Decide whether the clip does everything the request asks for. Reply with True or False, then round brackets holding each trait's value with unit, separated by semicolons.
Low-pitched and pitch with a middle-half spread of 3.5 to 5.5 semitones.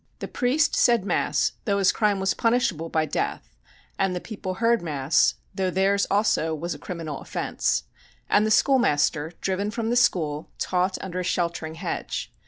False (185 Hz; 4.5 semitones)